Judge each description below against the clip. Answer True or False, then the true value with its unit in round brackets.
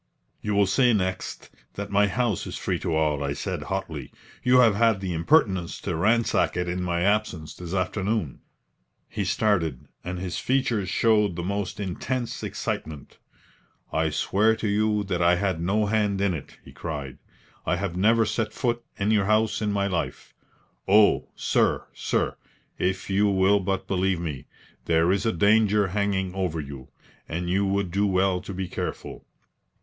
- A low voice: True (95 Hz)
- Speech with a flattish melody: False (3.1 semitones)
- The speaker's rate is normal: True (170 wpm)